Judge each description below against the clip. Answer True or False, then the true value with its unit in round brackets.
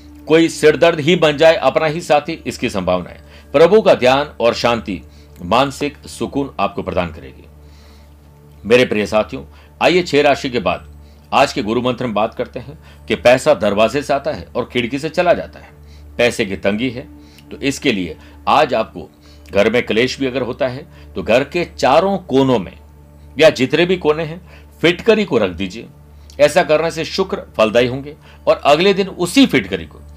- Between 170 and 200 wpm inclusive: True (185 wpm)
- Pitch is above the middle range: False (120 Hz)